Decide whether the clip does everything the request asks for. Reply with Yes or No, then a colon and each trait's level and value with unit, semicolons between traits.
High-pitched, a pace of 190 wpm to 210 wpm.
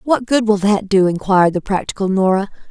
Yes: high, 200 Hz; average, 200 wpm